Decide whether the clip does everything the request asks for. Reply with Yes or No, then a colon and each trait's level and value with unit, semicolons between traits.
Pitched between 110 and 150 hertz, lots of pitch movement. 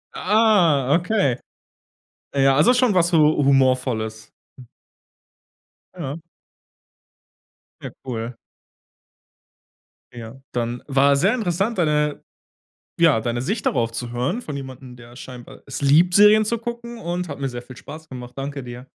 Yes: medium, 140 Hz; wide, 6.3 semitones